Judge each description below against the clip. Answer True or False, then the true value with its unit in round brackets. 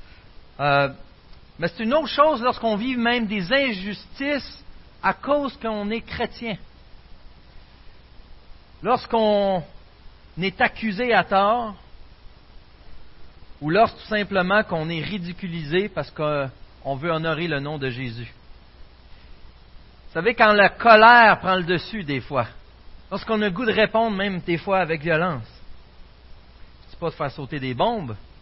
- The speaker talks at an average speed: False (135 wpm)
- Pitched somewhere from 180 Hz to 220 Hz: True (185 Hz)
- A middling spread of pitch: False (7.8 semitones)